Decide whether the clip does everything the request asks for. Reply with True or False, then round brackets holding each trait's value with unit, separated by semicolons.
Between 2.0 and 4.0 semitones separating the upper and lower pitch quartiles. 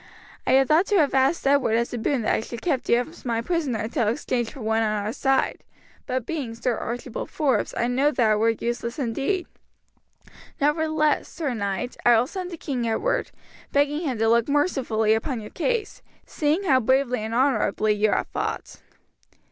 False (4.5 semitones)